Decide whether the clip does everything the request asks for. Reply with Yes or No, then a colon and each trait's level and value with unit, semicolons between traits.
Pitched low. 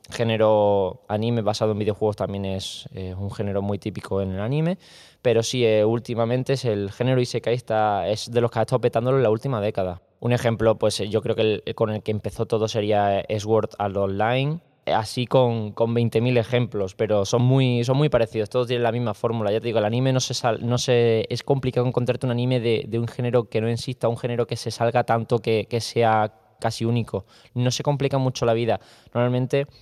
Yes: low, 115 Hz